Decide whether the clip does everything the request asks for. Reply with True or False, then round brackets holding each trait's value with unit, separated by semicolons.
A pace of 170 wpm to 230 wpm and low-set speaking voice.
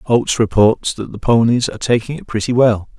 True (200 wpm; 115 Hz)